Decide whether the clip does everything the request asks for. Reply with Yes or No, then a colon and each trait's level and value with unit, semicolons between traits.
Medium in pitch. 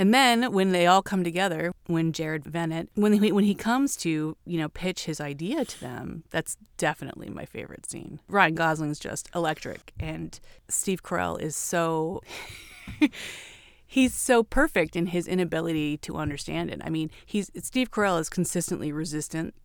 Yes: medium, 170 Hz